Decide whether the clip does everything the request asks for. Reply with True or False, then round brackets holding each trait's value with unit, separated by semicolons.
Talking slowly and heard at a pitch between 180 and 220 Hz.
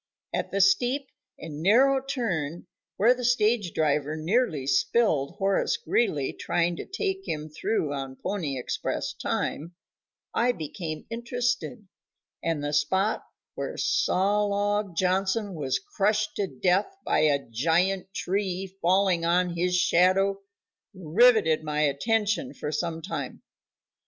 True (125 wpm; 185 Hz)